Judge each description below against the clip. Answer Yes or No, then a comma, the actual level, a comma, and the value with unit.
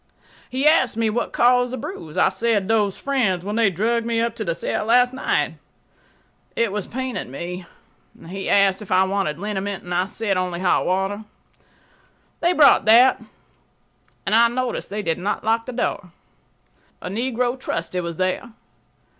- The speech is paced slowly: No, average, 165 wpm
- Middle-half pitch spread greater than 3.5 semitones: Yes, average, 4.1 semitones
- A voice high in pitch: Yes, high, 210 Hz